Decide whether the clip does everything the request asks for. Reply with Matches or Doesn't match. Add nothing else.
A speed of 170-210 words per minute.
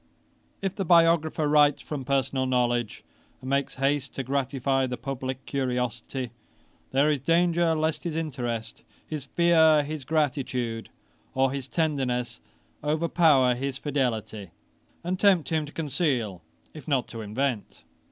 Doesn't match